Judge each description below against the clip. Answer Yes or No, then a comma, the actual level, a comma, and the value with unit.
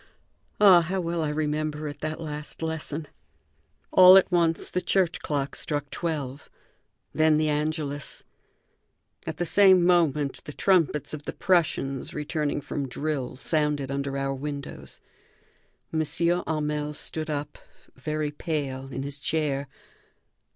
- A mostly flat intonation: Yes, narrow, 2.1 semitones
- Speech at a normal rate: No, slow, 130 wpm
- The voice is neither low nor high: Yes, medium, 150 Hz